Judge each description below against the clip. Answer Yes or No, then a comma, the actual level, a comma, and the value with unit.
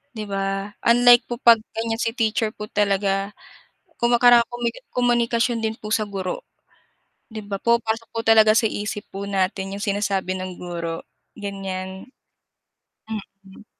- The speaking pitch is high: Yes, high, 210 Hz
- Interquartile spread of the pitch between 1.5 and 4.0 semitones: Yes, average, 2.8 semitones